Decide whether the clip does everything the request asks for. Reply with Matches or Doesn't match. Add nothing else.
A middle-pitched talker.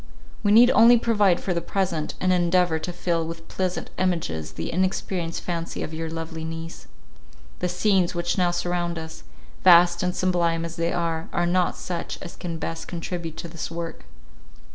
Matches